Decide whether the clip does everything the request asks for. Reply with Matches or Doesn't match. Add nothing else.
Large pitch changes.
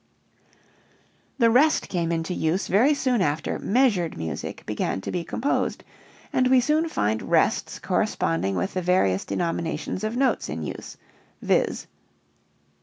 Matches